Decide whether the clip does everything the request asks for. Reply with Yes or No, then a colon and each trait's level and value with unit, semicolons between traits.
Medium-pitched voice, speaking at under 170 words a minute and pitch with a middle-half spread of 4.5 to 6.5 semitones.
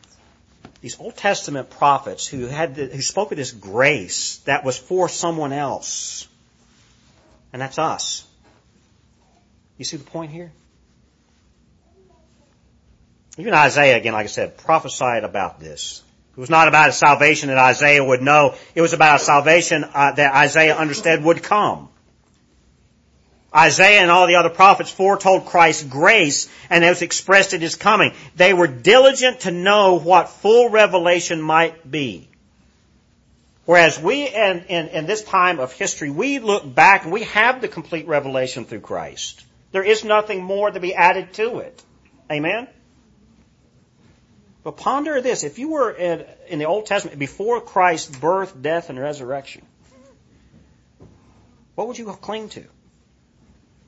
Yes: medium, 165 Hz; average, 150 wpm; wide, 5.4 semitones